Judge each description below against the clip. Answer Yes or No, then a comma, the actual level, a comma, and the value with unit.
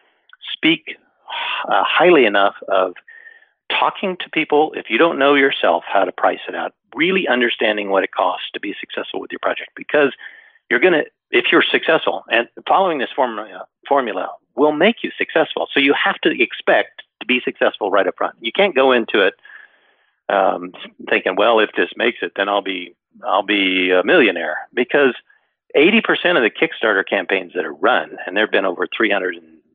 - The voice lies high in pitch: Yes, very high, 330 Hz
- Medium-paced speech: Yes, average, 180 wpm